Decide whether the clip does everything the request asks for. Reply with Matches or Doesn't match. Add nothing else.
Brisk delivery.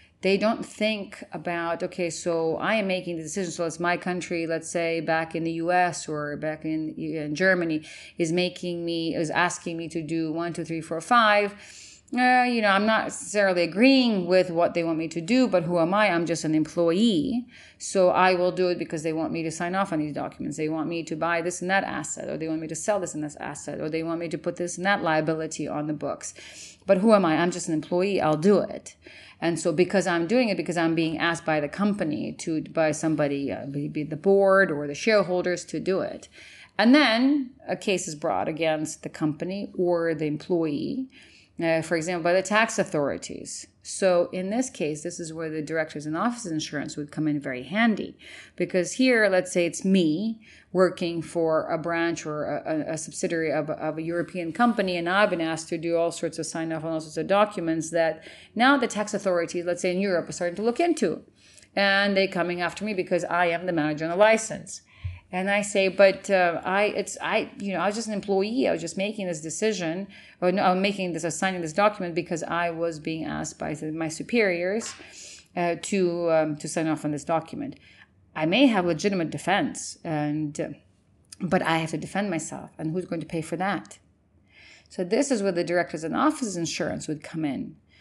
Matches